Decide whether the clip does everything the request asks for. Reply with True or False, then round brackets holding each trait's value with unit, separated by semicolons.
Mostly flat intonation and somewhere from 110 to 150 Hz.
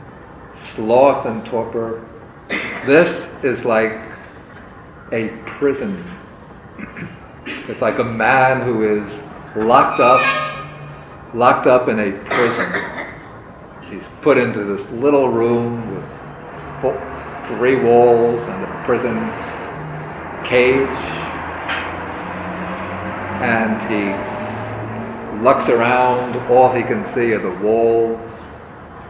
True (1.9 semitones; 115 Hz)